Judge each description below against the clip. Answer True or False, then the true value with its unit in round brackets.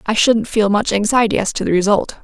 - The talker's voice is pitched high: True (215 Hz)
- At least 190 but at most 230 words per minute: False (240 wpm)